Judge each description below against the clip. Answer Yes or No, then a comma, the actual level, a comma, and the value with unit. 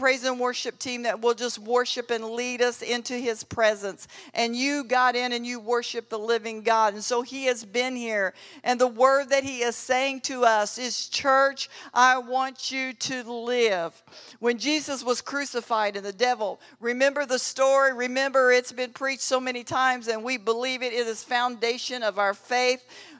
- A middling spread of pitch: No, narrow, 1.9 semitones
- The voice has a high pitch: Yes, high, 245 Hz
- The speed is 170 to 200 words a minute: Yes, average, 190 wpm